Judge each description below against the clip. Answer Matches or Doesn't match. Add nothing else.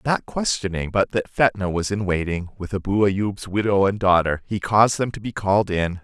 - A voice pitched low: Matches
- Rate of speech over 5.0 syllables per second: Matches